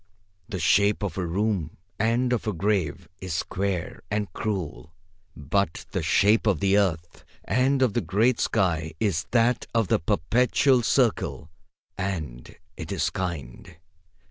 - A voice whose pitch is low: Yes, low, 100 Hz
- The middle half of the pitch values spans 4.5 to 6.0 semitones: Yes, average, 4.8 semitones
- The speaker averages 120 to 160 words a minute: Yes, average, 145 wpm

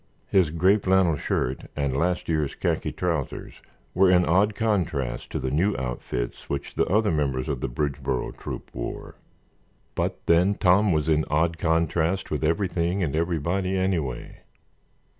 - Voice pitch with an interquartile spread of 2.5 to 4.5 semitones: Yes, average, 4.2 semitones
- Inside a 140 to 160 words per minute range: Yes, average, 150 wpm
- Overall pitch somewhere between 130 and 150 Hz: No, very low, 85 Hz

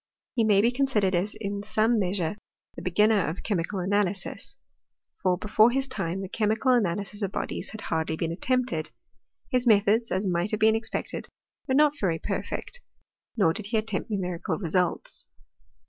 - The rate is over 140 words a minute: Yes, average, 160 wpm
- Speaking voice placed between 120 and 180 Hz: No, high, 205 Hz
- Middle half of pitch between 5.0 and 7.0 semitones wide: No, average, 3.4 semitones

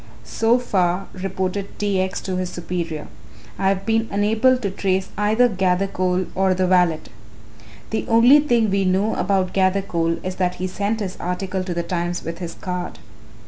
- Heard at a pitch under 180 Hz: No, high, 190 Hz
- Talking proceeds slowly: No, average, 170 wpm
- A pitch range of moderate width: No, narrow, 2.1 semitones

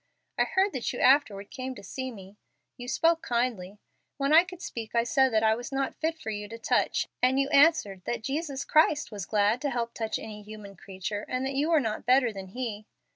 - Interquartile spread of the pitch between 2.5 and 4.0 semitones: No, average, 4.5 semitones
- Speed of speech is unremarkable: No, fast, 225 wpm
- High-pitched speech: Yes, high, 245 Hz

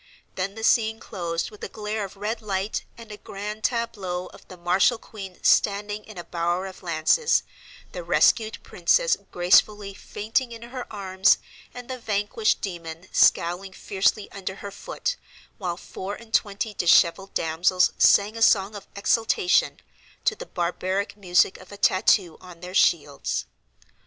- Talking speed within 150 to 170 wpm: Yes, average, 155 wpm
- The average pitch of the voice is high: Yes, high, 200 Hz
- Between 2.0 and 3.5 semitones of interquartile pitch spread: Yes, average, 3.1 semitones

